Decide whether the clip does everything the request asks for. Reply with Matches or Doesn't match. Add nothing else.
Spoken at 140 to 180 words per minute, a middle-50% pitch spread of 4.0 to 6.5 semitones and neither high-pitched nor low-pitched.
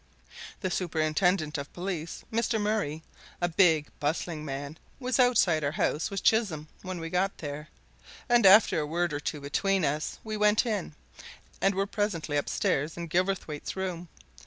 Matches